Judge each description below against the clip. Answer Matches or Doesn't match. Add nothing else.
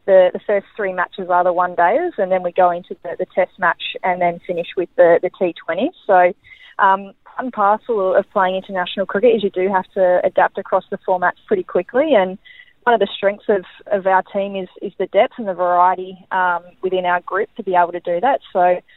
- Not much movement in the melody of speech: Matches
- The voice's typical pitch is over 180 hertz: Matches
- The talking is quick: Matches